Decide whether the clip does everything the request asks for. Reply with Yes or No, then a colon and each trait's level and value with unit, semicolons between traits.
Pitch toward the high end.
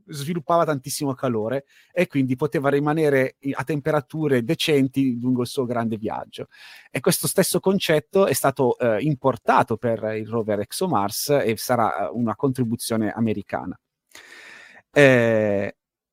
No: low, 135 Hz